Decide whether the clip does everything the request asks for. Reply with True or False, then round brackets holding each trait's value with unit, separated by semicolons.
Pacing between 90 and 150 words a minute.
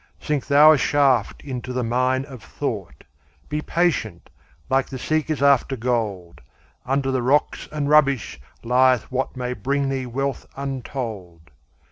True (140 wpm)